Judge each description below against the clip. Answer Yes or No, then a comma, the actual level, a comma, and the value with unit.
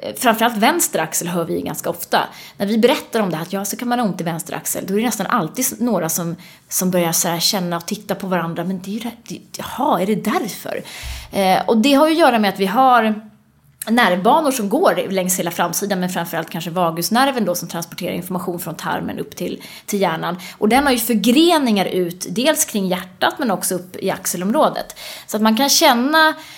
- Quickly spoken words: Yes, fast, 215 wpm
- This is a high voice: Yes, high, 200 Hz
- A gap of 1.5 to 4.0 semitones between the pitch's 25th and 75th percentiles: No, average, 5.1 semitones